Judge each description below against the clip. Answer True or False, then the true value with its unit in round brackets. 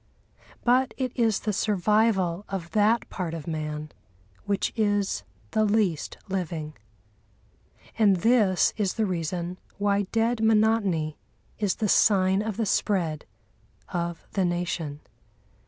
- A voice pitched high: True (195 Hz)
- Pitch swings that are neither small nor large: True (4.0 semitones)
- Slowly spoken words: True (120 wpm)